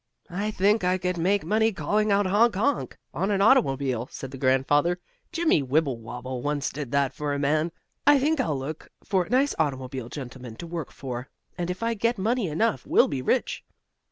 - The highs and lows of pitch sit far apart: Yes, wide, 7.6 semitones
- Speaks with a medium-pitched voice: Yes, medium, 170 Hz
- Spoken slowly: No, average, 190 wpm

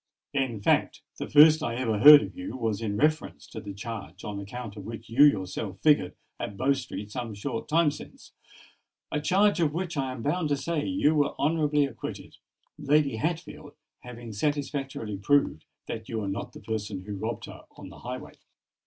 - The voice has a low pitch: Yes, low, 130 Hz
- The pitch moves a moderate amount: No, wide, 5.7 semitones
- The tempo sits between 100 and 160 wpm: No, average, 185 wpm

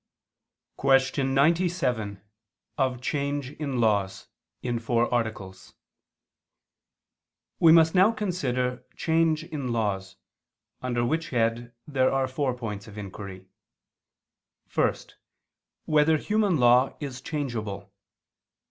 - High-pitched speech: No, low, 130 Hz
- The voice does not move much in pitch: No, average, 4.7 semitones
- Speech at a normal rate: No, slow, 105 wpm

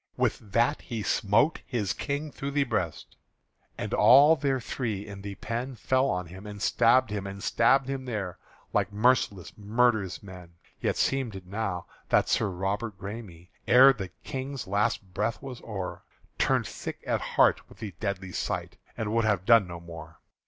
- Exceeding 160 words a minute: Yes, average, 170 wpm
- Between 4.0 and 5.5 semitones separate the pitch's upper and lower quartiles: Yes, average, 4.3 semitones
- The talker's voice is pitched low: Yes, low, 105 Hz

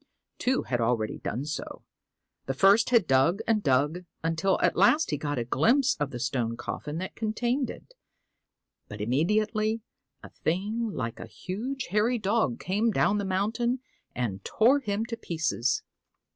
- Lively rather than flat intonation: Yes, wide, 9.0 semitones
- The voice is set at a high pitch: Yes, high, 195 Hz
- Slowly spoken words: No, average, 160 wpm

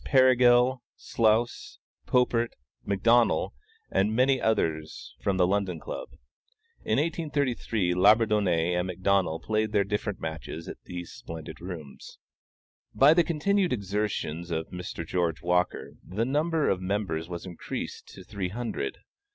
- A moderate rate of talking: No, slow, 125 wpm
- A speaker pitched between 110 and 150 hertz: No, low, 100 Hz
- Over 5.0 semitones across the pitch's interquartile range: Yes, wide, 5.4 semitones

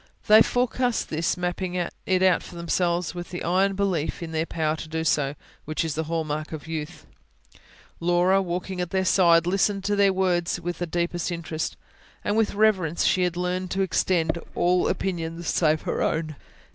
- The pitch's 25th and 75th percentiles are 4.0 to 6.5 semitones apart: No, narrow, 2.5 semitones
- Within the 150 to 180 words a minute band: No, average, 190 wpm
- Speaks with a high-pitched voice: No, medium, 175 Hz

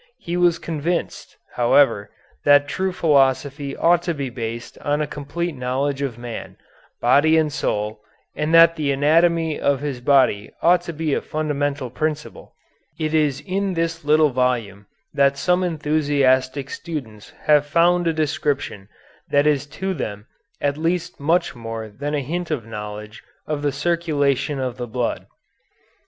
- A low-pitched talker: No, medium, 145 Hz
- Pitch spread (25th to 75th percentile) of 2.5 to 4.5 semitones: Yes, average, 3.9 semitones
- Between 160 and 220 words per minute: No, average, 150 wpm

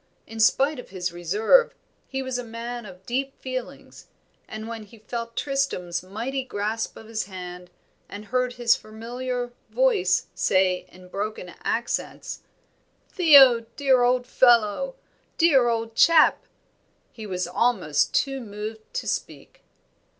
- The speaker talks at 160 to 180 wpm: No, slow, 135 wpm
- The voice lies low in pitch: No, high, 230 Hz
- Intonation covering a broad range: No, average, 3.9 semitones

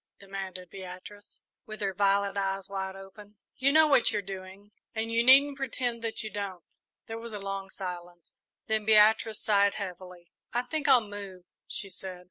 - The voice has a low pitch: No, high, 200 Hz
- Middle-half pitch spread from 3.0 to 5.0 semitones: No, narrow, 2.5 semitones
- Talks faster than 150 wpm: Yes, average, 170 wpm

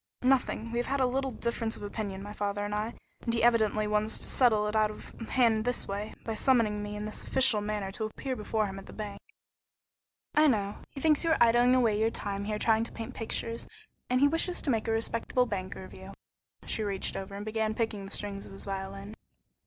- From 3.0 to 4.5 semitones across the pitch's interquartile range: No, narrow, 2.6 semitones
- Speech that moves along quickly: Yes, fast, 230 wpm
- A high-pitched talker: Yes, high, 215 Hz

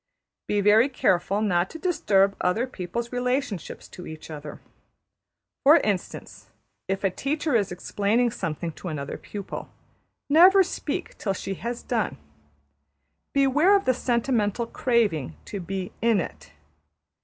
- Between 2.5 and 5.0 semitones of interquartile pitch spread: No, wide, 5.5 semitones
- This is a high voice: Yes, high, 210 Hz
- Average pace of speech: No, slow, 130 wpm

